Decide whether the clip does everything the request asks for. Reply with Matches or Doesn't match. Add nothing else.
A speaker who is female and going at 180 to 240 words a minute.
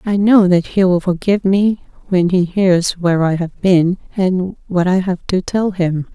Matches